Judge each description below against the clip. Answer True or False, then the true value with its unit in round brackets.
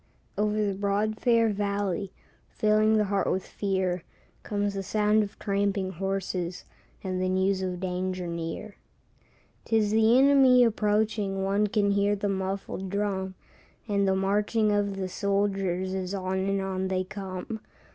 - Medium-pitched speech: False (200 Hz)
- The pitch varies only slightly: True (1.8 semitones)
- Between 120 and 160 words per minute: True (150 wpm)